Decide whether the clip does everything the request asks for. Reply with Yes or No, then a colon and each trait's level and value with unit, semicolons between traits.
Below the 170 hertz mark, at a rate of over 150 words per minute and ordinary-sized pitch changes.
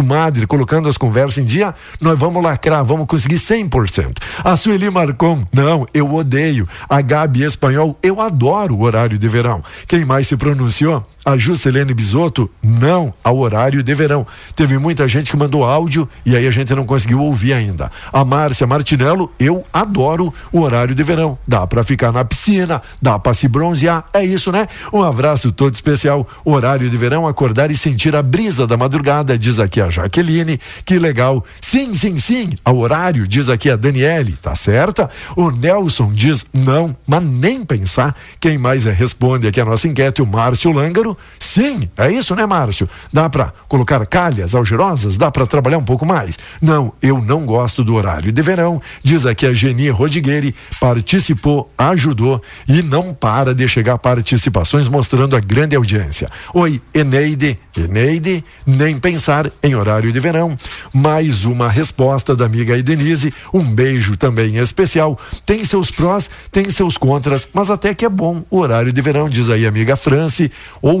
Yes: medium, 140 Hz; average, 170 wpm; average, 4.5 semitones